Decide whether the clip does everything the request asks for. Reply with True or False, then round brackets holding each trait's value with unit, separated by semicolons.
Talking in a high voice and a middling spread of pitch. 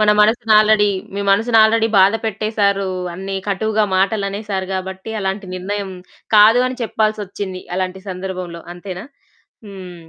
False (200 Hz; 2.3 semitones)